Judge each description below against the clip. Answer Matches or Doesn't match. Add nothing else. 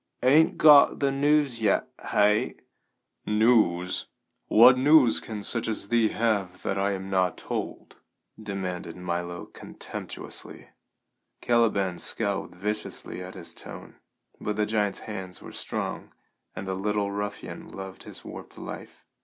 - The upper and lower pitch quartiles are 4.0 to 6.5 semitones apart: Doesn't match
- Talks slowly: Matches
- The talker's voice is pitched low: Matches